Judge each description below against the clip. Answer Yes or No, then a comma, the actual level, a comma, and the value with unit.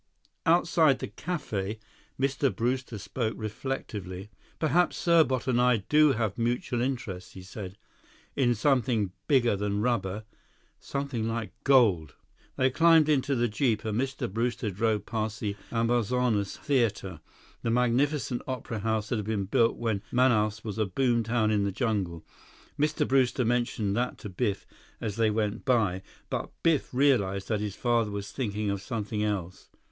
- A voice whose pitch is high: No, low, 115 Hz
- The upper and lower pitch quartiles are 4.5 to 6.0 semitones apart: No, average, 3.8 semitones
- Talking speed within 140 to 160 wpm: Yes, average, 150 wpm